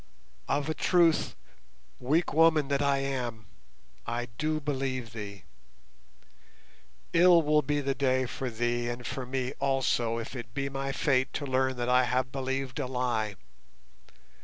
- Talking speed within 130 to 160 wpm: Yes, average, 150 wpm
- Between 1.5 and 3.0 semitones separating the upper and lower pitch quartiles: Yes, narrow, 2.5 semitones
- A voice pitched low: Yes, low, 130 Hz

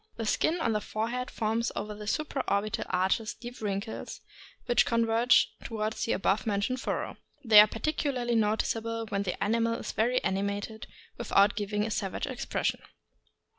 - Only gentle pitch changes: Yes, narrow, 2.2 semitones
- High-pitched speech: Yes, high, 220 Hz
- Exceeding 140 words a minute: Yes, average, 155 wpm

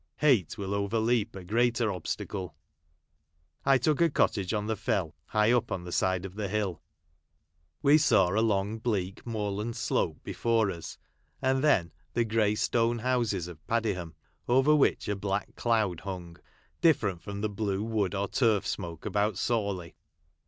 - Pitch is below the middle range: Yes, low, 105 Hz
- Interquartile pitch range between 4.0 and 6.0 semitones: No, average, 3.4 semitones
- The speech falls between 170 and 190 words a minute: No, average, 160 wpm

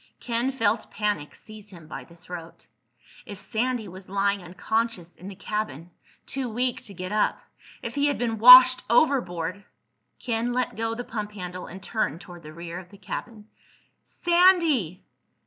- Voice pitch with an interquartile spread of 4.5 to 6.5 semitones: Yes, average, 5.0 semitones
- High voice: Yes, high, 210 Hz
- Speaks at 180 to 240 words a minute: No, average, 160 wpm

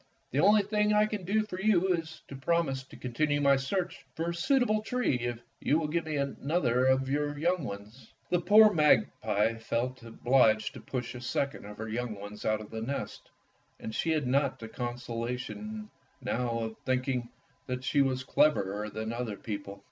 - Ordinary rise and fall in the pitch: No, wide, 6.6 semitones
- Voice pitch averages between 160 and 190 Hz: No, low, 130 Hz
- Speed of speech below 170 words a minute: No, average, 190 wpm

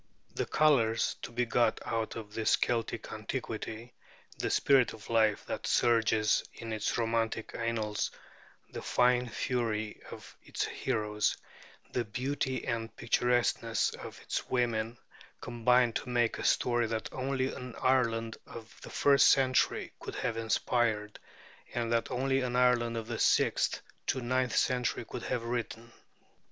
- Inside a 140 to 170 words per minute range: Yes, average, 145 wpm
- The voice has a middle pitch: No, low, 115 Hz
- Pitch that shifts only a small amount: Yes, narrow, 1.7 semitones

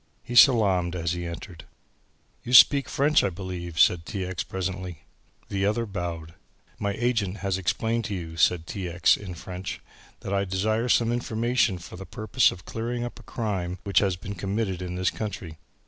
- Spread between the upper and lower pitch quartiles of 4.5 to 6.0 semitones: No, average, 3.7 semitones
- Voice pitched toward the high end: No, very low, 95 Hz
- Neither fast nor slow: Yes, average, 180 wpm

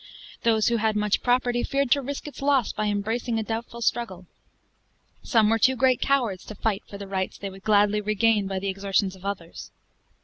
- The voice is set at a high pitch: Yes, high, 215 Hz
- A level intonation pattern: No, average, 3.2 semitones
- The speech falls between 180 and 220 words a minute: Yes, average, 200 wpm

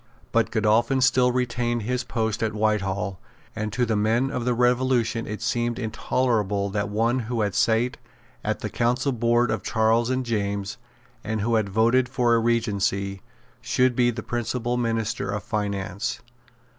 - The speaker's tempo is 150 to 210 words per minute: Yes, average, 160 wpm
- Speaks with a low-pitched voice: Yes, low, 115 Hz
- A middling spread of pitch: No, narrow, 2.3 semitones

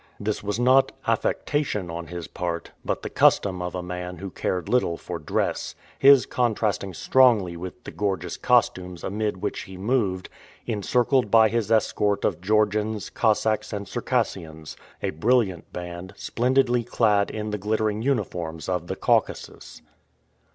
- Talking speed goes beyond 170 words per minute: No, average, 145 wpm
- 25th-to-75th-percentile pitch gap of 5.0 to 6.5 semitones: No, average, 4.3 semitones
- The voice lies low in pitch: Yes, low, 105 Hz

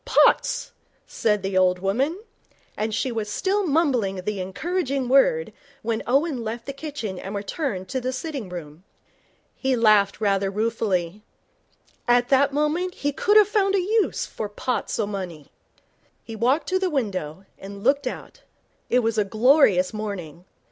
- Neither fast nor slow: Yes, average, 155 wpm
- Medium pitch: No, high, 230 Hz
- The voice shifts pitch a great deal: Yes, wide, 6.5 semitones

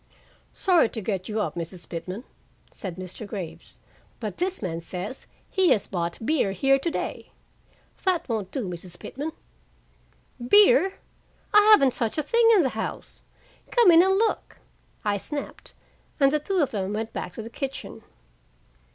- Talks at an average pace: Yes, average, 160 wpm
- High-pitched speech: Yes, high, 235 Hz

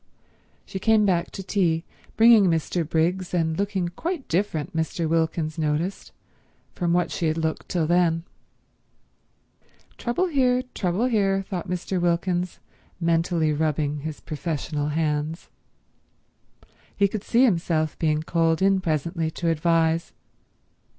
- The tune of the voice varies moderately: Yes, average, 3.1 semitones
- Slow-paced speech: Yes, slow, 125 wpm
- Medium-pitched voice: Yes, medium, 170 Hz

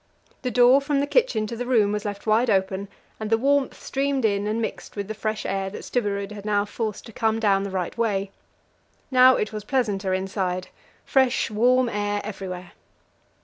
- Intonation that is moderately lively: Yes, average, 3.6 semitones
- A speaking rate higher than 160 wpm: Yes, average, 190 wpm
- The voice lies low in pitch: No, high, 215 Hz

